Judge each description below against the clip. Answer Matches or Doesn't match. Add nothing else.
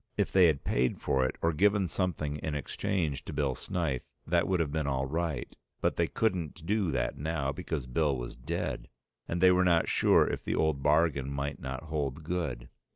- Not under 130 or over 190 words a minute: Doesn't match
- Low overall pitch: Matches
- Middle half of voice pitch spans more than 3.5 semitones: Matches